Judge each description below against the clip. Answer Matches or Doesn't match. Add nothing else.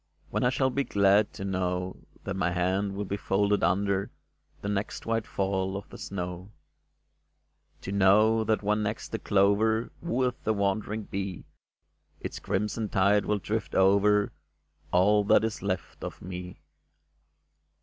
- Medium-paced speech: Matches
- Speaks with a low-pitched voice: Matches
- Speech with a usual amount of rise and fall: Doesn't match